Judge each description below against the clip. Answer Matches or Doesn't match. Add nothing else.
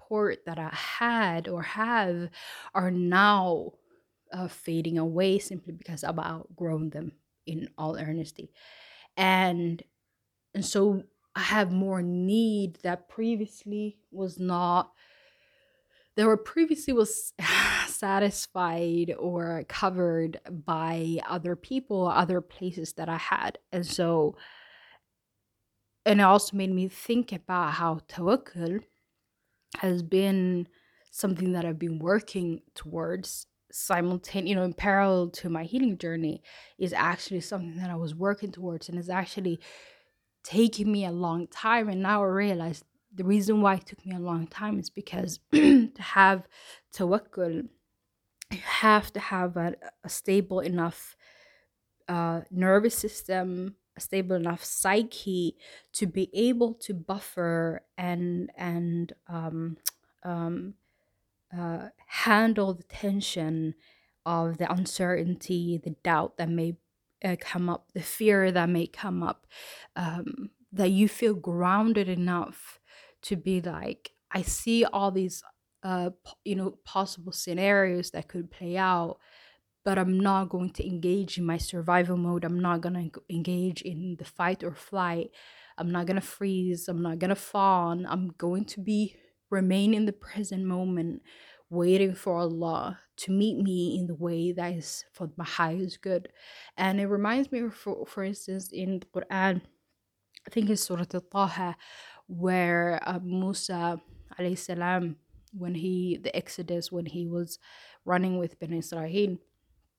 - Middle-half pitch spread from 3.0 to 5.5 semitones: Doesn't match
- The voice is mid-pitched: Matches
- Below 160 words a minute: Matches